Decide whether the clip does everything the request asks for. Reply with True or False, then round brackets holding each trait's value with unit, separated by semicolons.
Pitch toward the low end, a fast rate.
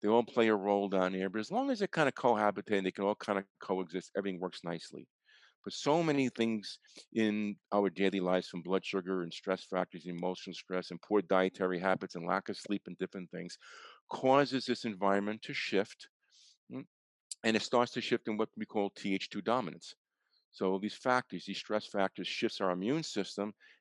False (100 Hz; 195 wpm)